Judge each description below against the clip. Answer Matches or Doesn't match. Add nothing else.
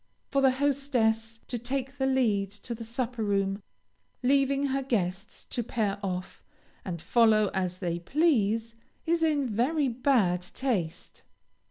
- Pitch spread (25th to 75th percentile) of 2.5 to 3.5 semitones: Doesn't match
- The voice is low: Doesn't match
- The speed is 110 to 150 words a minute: Matches